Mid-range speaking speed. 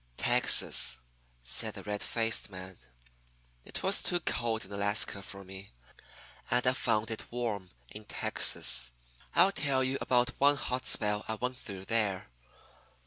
Yes: average, 145 wpm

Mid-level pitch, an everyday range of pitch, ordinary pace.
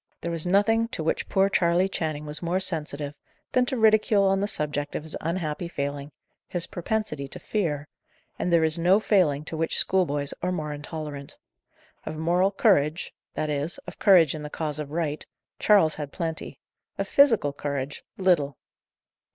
Yes: medium, 160 Hz; average, 4.1 semitones; average, 170 wpm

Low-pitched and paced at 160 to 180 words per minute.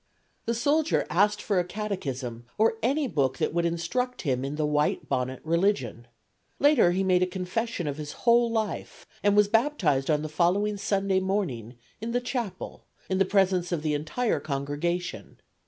No: medium, 185 Hz; average, 170 wpm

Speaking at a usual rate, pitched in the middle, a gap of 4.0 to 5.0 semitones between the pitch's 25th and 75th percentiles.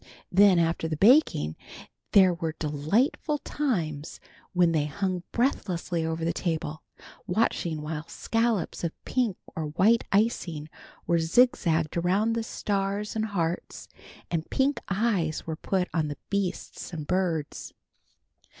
No: slow, 130 wpm; medium, 175 Hz; average, 4.4 semitones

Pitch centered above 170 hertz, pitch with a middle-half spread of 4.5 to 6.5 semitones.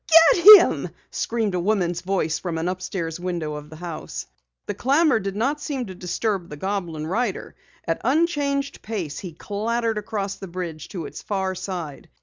Yes: high, 190 Hz; average, 4.9 semitones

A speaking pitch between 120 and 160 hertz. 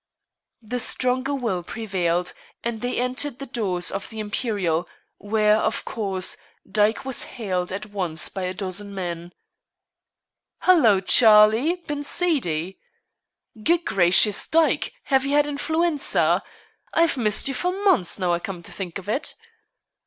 No: high, 215 Hz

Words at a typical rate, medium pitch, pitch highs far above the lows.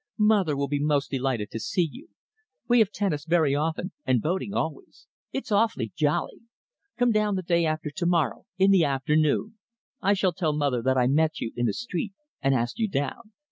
Yes: average, 195 wpm; medium, 160 Hz; wide, 6.0 semitones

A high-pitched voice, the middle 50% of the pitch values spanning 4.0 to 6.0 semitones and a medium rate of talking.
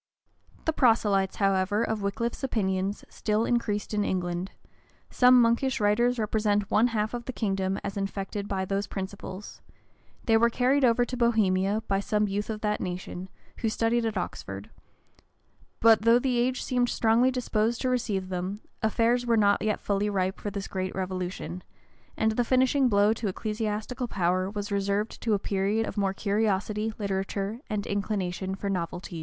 No: high, 210 Hz; average, 2.9 semitones; average, 165 wpm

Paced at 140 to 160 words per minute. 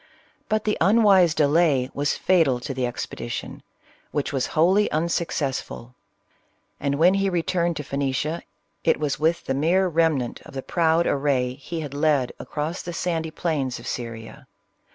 Yes: average, 155 wpm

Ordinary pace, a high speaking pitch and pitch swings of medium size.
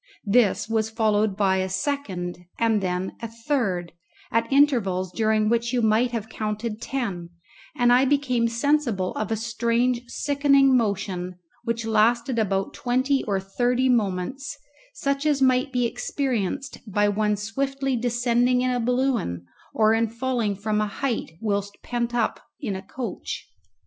Yes: average, 150 wpm; high, 230 Hz; average, 3.5 semitones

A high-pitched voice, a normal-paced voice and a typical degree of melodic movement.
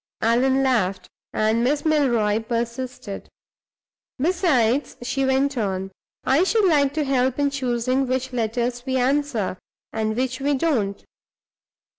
No: very high, 255 Hz; slow, 125 wpm; average, 3.3 semitones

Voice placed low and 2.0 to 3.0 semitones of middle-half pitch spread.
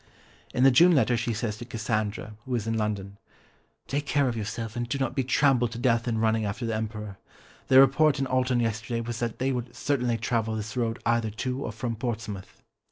Yes: low, 115 Hz; narrow, 2.6 semitones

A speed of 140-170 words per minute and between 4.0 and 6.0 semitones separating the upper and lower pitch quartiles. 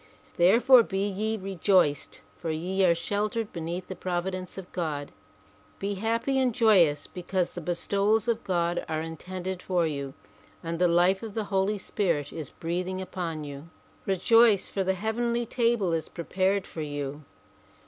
No: average, 160 wpm; average, 3.5 semitones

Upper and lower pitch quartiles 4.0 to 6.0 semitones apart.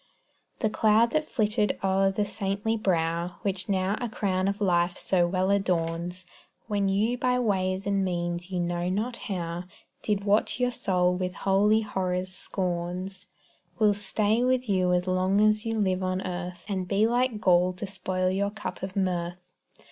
No: narrow, 2.5 semitones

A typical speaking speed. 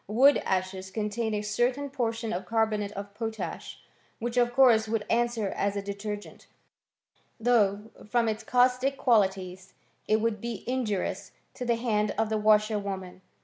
Yes: average, 150 wpm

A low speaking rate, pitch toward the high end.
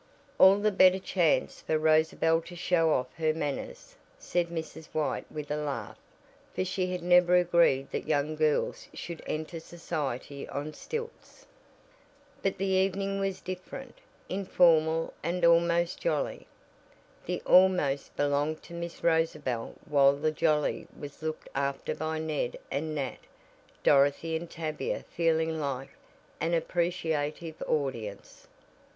No: slow, 130 wpm; medium, 160 Hz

